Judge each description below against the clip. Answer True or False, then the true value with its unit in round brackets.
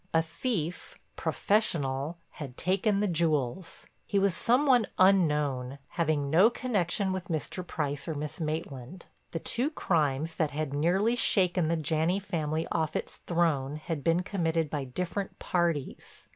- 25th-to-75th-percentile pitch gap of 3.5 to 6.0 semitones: True (4.0 semitones)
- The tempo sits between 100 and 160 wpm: True (145 wpm)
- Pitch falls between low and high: True (165 Hz)